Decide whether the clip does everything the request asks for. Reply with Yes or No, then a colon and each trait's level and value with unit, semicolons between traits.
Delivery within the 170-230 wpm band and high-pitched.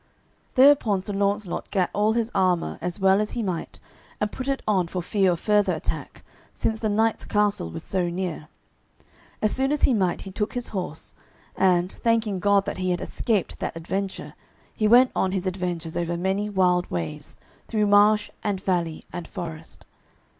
Yes: average, 180 wpm; high, 195 Hz